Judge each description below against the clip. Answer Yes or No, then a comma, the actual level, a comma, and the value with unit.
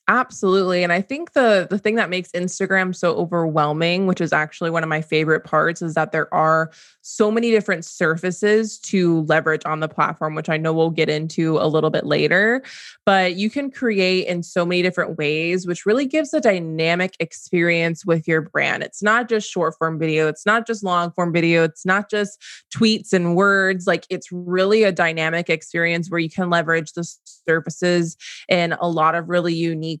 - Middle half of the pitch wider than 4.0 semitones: No, average, 3.0 semitones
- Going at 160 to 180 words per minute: No, average, 195 wpm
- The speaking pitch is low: No, medium, 175 Hz